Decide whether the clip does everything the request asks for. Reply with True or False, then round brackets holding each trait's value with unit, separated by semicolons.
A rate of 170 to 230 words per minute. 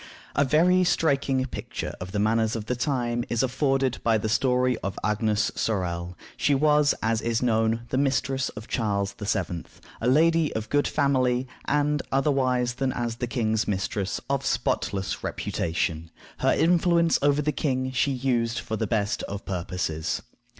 False (160 wpm)